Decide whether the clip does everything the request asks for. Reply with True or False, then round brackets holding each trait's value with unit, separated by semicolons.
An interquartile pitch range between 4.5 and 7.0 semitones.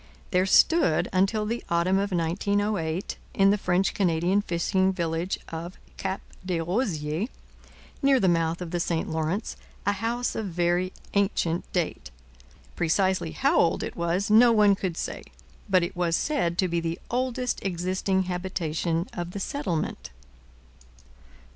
False (2.9 semitones)